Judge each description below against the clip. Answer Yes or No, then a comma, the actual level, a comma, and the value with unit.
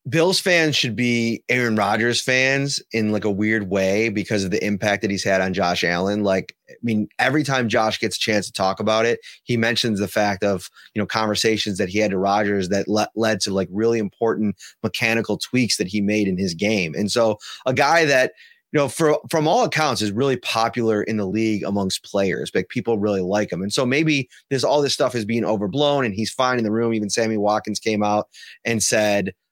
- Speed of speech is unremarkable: No, fast, 225 wpm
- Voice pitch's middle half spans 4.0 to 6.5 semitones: No, average, 3.1 semitones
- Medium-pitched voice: No, low, 110 Hz